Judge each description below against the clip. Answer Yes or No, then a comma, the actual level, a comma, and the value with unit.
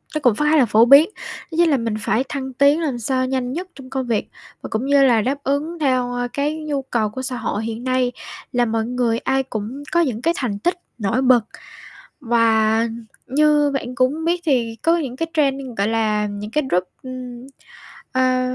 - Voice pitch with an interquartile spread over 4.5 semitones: No, average, 3.6 semitones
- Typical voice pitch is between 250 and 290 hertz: Yes, very high, 255 Hz